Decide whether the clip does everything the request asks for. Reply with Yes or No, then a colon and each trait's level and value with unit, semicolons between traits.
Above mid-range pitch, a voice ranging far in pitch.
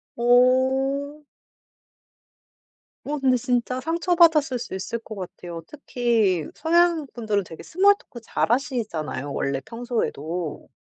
Yes: high, 245 Hz; wide, 6.1 semitones